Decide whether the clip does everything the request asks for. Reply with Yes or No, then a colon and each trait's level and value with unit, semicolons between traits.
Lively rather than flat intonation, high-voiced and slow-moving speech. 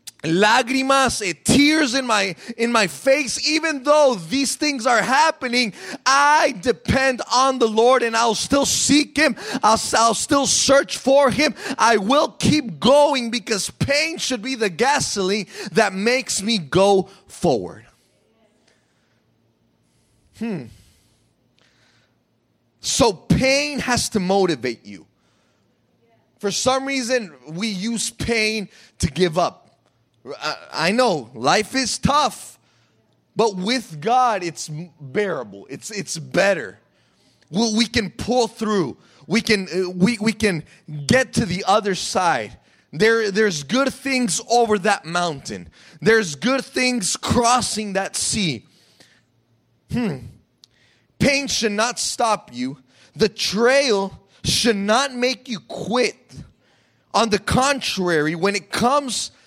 Yes: wide, 5.8 semitones; high, 220 Hz; slow, 120 wpm